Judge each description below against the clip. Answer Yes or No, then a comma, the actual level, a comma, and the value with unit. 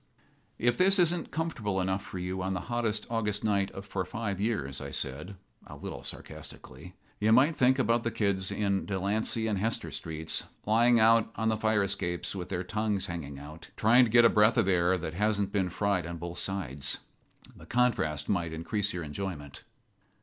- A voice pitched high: No, low, 100 Hz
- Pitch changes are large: No, average, 3.9 semitones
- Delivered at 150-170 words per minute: No, average, 185 wpm